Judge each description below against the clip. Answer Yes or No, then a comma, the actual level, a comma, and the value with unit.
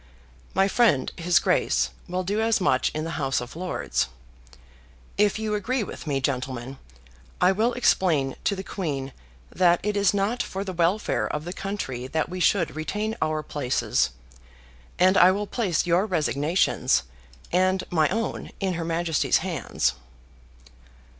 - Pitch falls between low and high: Yes, medium, 180 Hz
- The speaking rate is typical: Yes, average, 155 wpm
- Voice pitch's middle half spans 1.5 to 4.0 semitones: No, average, 4.7 semitones